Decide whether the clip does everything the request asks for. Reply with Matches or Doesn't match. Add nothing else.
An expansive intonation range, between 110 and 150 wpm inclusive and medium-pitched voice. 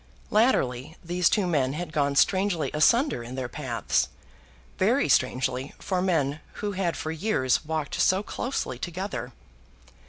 Matches